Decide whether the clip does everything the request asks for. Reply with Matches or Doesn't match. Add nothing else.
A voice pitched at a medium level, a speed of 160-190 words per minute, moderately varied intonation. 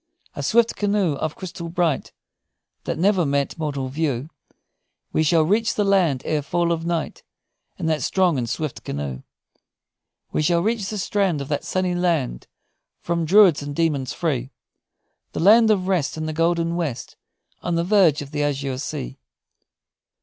Matches